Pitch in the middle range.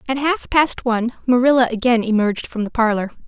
No: high, 240 Hz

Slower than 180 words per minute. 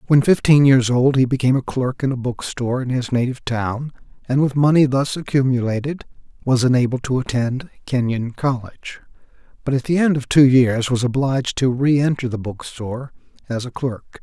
No: average, 185 wpm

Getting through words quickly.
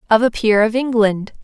Yes: fast, 210 wpm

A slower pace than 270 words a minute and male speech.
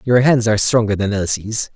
Yes: fast, 205 wpm; male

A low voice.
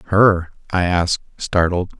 Yes: very low, 90 Hz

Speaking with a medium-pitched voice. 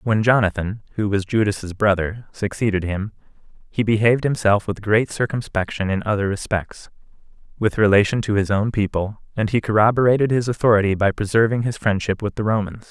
No: low, 105 Hz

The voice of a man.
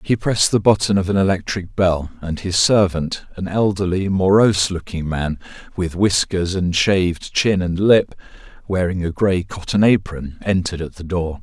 Yes: male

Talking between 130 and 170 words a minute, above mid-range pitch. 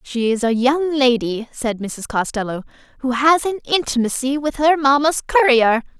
Yes: average, 160 wpm; very high, 260 Hz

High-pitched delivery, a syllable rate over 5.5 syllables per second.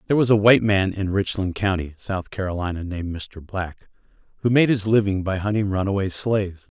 No: low, 100 Hz; 5.8 syllables/s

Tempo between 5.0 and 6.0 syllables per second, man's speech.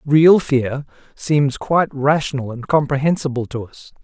No: 4.5 syllables/s; male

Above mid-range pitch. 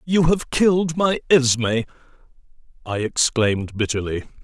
No: low, 135 Hz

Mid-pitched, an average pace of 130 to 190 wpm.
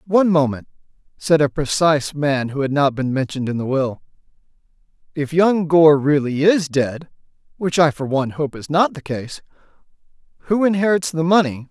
Yes: medium, 150 Hz; average, 160 wpm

